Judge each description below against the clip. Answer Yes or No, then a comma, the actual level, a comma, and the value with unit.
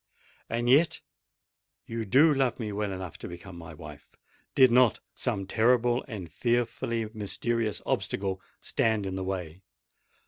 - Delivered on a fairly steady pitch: No, average, 4.1 semitones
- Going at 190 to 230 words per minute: No, slow, 135 wpm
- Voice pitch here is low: Yes, low, 110 Hz